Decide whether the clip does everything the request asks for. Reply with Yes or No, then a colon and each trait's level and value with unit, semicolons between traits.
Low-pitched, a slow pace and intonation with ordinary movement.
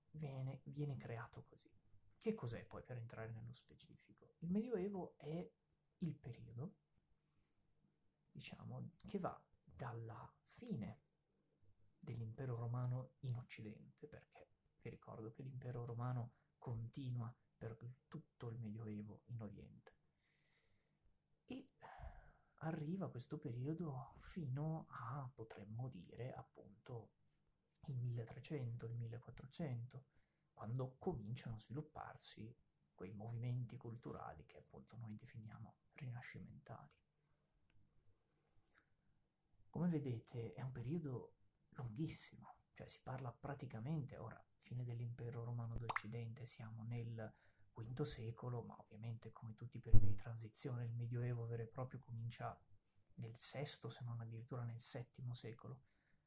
Yes: low, 120 Hz; slow, 110 wpm; average, 3.1 semitones